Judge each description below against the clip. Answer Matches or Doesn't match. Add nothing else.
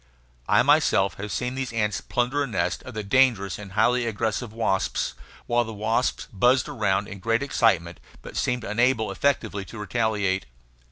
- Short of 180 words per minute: Matches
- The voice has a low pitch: Matches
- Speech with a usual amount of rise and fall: Matches